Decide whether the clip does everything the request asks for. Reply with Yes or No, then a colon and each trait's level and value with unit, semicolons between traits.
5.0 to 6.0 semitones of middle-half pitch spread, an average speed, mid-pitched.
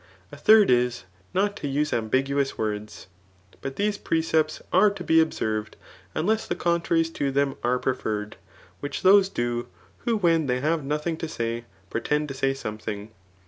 Yes: wide, 5.6 semitones; average, 170 wpm; medium, 145 Hz